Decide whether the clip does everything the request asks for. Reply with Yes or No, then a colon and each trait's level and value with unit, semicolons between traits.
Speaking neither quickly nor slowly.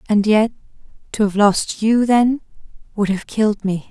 Yes: average, 170 wpm